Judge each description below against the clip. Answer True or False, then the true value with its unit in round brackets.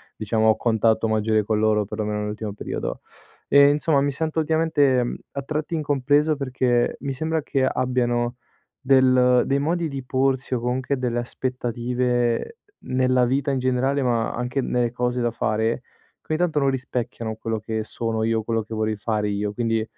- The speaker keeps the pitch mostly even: False (3.4 semitones)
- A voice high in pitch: False (125 Hz)